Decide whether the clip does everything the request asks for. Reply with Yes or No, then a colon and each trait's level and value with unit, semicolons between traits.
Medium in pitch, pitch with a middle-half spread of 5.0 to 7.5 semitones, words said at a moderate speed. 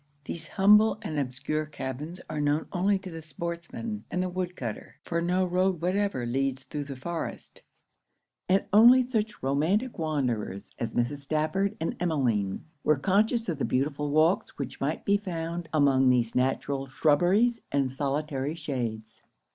Yes: medium, 155 Hz; average, 5.3 semitones; average, 150 wpm